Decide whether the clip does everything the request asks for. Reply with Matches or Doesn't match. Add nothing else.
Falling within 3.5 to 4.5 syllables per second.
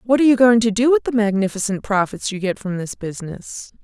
Doesn't match